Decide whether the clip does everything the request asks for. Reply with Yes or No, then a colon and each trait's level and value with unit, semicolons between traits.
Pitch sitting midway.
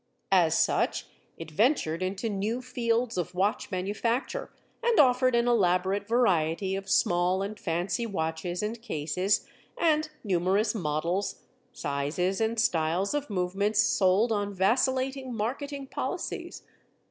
No: high, 200 Hz